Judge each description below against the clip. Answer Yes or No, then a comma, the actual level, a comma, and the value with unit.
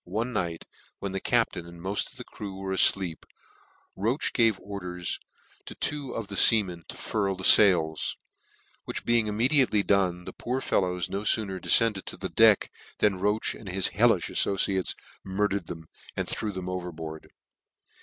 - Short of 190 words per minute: Yes, average, 165 wpm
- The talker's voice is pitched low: Yes, very low, 95 Hz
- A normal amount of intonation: Yes, average, 3.1 semitones